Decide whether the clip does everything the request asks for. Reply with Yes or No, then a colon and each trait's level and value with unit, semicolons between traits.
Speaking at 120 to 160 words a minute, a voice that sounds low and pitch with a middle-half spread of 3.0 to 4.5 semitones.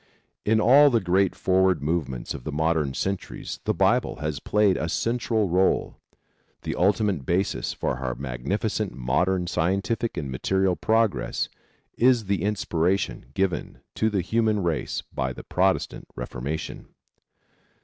No: slow, 135 wpm; very low, 95 Hz; average, 5.2 semitones